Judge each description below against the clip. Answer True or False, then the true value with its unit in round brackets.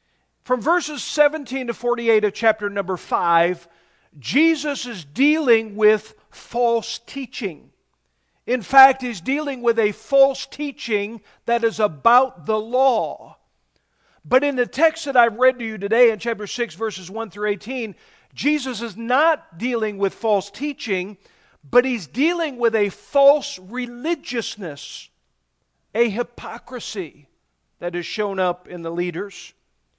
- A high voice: True (235 Hz)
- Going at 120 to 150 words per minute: True (135 wpm)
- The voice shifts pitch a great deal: False (4.1 semitones)